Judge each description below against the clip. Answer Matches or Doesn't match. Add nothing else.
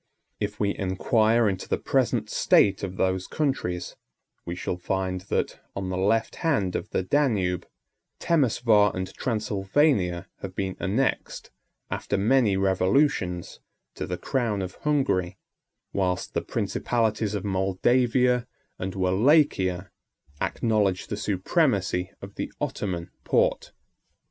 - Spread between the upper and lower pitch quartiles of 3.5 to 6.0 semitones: Matches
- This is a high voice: Doesn't match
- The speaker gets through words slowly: Matches